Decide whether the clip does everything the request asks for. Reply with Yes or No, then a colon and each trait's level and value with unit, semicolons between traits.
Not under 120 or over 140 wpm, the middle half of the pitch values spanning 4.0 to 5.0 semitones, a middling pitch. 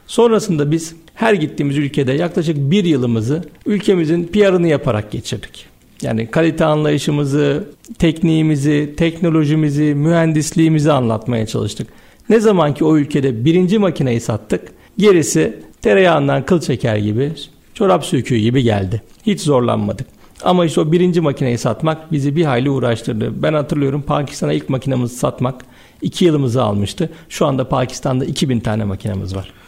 Yes: average, 130 wpm; average, 4.4 semitones; medium, 150 Hz